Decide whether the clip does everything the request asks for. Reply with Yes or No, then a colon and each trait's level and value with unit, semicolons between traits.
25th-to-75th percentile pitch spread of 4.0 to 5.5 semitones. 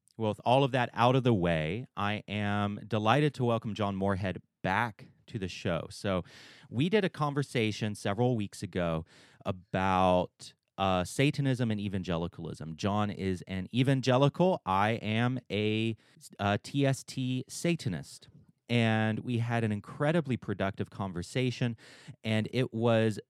Yes: average, 4.4 semitones